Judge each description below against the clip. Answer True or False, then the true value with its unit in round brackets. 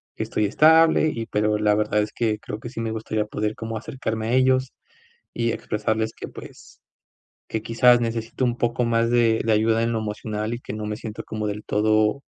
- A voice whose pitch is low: True (110 Hz)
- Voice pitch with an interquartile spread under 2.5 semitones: True (1.7 semitones)